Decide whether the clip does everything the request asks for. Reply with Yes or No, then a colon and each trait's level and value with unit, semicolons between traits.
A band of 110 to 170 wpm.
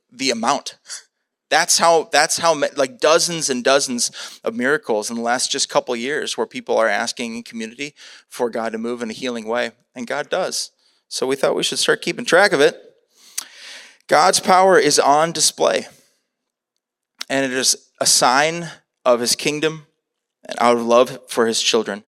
No: average, 180 wpm